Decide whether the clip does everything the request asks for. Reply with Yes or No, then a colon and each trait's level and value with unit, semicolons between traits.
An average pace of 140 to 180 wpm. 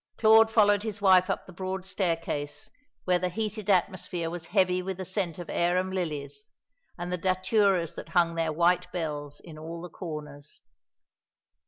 Yes: average, 165 wpm